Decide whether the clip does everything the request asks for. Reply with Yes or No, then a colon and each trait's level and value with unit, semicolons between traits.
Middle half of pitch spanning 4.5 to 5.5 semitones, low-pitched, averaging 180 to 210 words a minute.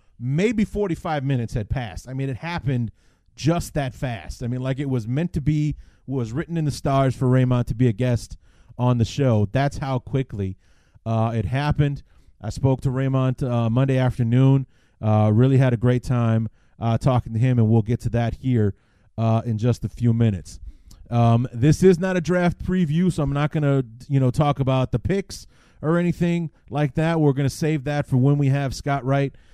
No: average, 3.8 semitones; low, 130 Hz; fast, 205 wpm